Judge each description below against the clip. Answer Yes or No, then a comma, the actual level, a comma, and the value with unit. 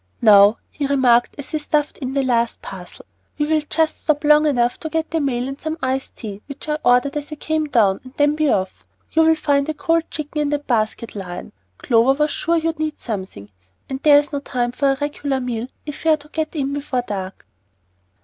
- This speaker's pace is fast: Yes, fast, 215 wpm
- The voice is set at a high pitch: Yes, very high, 280 Hz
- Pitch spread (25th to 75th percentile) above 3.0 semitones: Yes, average, 4.0 semitones